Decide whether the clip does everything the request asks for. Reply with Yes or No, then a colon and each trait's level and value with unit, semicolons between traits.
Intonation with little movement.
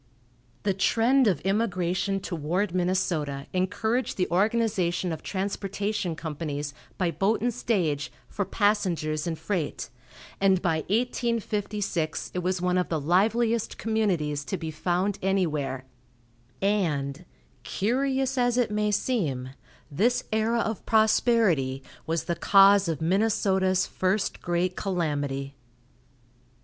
No: average, 4.5 semitones